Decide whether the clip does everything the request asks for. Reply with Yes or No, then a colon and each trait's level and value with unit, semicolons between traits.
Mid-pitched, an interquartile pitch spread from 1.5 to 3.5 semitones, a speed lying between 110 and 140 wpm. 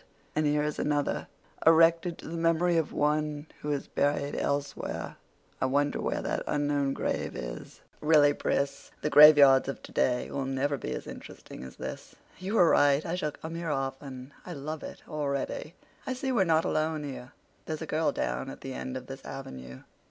No: medium, 145 Hz; narrow, 2.6 semitones; average, 180 wpm